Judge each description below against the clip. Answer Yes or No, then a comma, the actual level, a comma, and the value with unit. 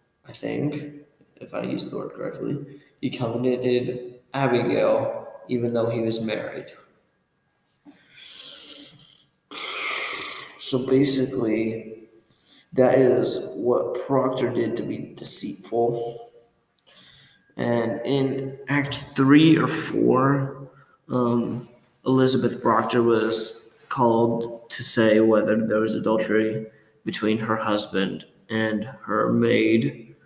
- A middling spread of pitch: Yes, average, 3.2 semitones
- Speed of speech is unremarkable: No, slow, 95 wpm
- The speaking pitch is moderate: No, low, 120 Hz